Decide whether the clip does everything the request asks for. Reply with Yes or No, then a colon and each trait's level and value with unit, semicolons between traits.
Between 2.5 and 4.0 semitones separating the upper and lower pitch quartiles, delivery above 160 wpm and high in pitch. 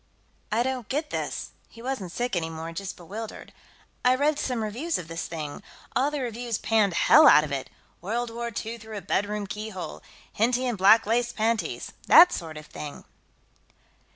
No: average, 4.6 semitones; average, 175 wpm; high, 220 Hz